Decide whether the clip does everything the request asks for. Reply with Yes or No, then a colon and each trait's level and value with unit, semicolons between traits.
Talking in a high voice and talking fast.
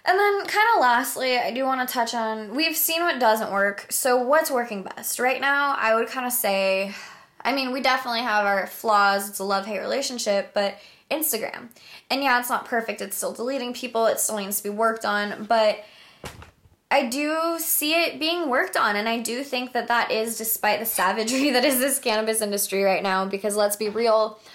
Yes: high, 235 Hz; fast, 210 wpm